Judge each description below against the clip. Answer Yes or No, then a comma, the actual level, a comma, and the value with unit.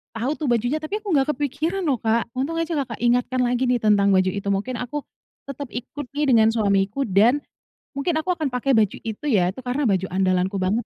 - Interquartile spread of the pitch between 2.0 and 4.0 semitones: No, wide, 5.5 semitones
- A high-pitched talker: Yes, high, 245 Hz